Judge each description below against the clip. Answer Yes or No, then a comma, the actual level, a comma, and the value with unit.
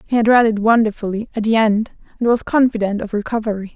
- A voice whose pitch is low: No, high, 220 Hz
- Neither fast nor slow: Yes, average, 190 wpm